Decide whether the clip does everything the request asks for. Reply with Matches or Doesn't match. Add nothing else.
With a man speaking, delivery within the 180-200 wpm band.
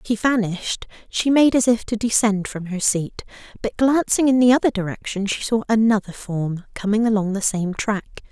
Doesn't match